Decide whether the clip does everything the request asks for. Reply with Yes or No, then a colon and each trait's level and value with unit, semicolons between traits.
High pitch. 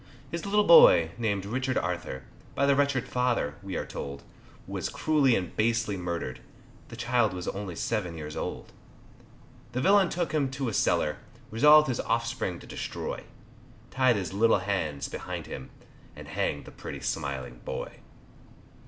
No: low, 110 Hz